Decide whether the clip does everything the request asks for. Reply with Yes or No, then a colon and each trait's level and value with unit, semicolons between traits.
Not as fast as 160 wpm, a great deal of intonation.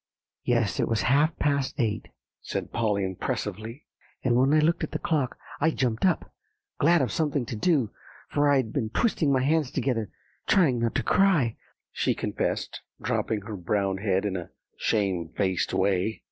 No: average, 165 wpm; wide, 5.7 semitones